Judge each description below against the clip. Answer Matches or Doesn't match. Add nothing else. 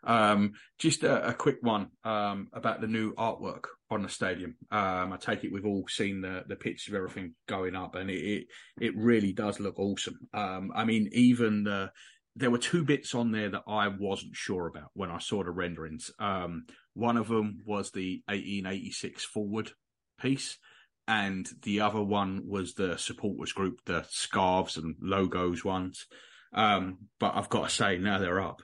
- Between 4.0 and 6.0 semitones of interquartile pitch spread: Doesn't match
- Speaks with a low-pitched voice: Matches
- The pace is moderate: Matches